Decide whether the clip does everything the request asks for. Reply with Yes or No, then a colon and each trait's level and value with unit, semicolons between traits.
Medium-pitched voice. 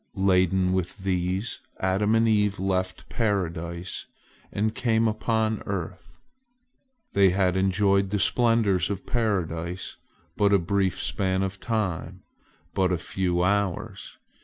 No: very low, 95 Hz